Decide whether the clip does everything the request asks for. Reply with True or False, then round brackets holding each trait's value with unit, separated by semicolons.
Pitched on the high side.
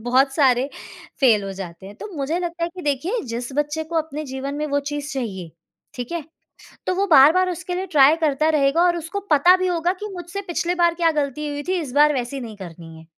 True (295 Hz)